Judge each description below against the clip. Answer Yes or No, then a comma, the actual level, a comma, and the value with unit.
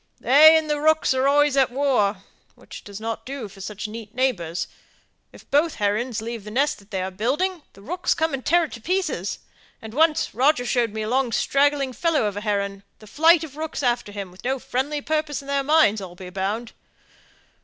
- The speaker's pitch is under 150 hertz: No, very high, 255 Hz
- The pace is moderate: No, fast, 210 wpm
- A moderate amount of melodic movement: No, wide, 6.1 semitones